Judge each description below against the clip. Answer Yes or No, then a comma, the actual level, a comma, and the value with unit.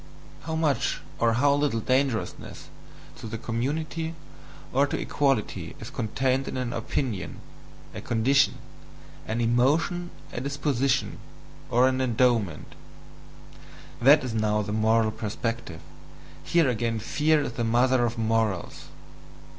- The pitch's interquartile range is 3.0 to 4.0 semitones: Yes, average, 3.7 semitones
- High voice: No, low, 120 Hz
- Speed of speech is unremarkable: No, slow, 125 wpm